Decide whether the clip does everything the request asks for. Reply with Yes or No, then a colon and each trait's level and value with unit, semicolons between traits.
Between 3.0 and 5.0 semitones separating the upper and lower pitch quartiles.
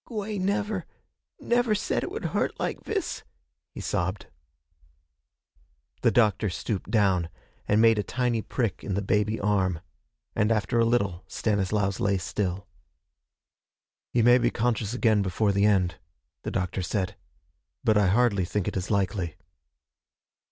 Yes: average, 3.4 semitones